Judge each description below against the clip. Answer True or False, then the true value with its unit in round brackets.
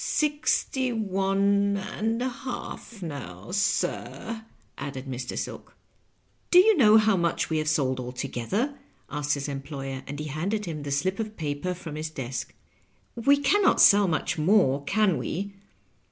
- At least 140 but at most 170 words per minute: True (165 wpm)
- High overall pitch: False (180 Hz)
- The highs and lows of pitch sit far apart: True (7.2 semitones)